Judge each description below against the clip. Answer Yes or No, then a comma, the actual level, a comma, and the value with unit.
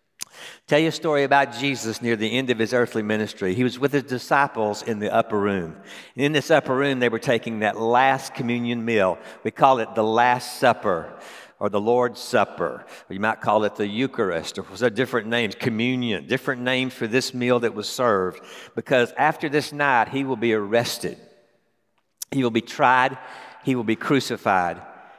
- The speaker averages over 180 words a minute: Yes, average, 190 wpm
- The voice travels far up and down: No, average, 3.0 semitones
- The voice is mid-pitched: No, low, 125 Hz